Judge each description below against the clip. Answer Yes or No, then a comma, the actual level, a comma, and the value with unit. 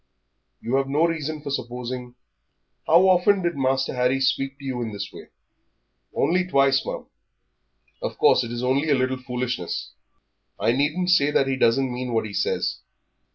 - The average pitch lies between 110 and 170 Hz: Yes, low, 135 Hz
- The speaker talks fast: No, average, 170 wpm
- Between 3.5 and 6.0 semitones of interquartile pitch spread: No, average, 2.9 semitones